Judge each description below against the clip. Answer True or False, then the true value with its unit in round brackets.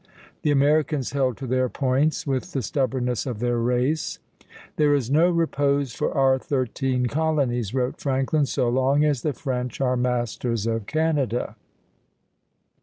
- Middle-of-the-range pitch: False (130 Hz)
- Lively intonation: False (2.7 semitones)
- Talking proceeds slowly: False (145 wpm)